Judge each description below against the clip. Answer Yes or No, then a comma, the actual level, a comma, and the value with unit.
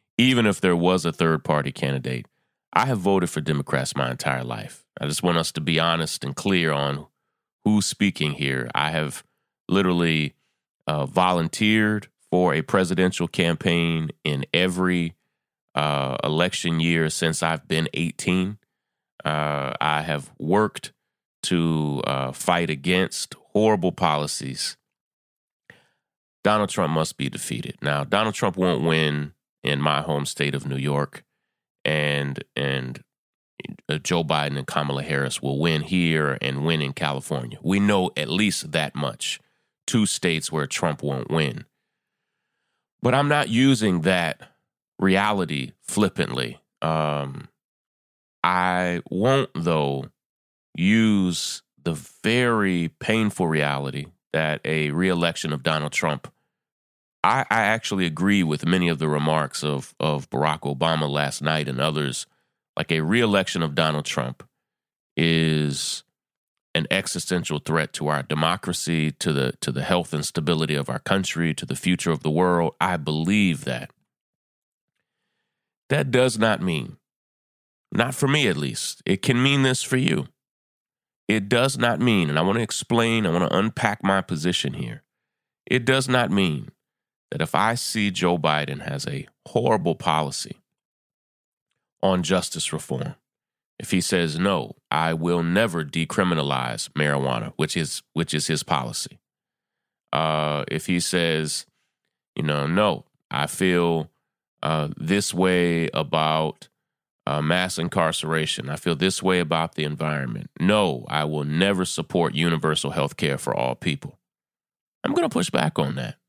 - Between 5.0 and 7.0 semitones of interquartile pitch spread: No, average, 3.7 semitones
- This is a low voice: Yes, very low, 80 Hz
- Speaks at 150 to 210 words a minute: No, average, 140 wpm